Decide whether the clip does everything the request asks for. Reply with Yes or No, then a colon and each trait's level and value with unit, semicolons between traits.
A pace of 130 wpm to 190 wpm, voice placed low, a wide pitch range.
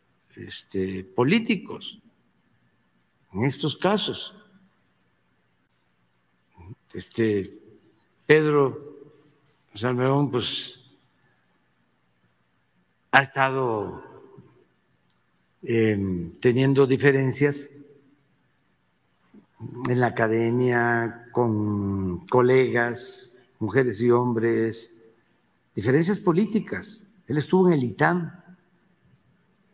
No: slow, 60 wpm; low, 125 Hz; wide, 6.2 semitones